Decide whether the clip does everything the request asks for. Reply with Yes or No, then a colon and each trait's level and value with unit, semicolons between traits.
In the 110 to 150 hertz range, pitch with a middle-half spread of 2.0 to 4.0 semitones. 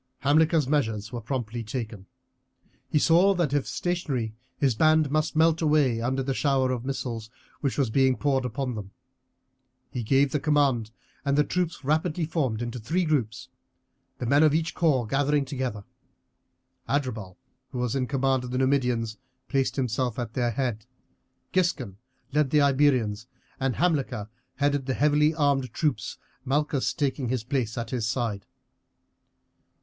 Yes: low, 135 Hz; average, 3.7 semitones